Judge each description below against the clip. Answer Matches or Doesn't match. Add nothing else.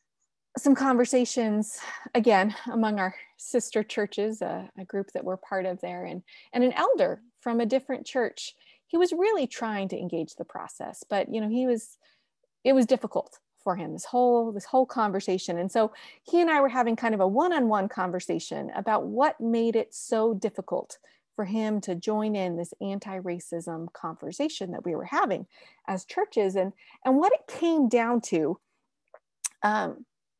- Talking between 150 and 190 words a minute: Matches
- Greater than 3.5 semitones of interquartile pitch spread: Matches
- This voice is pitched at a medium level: Doesn't match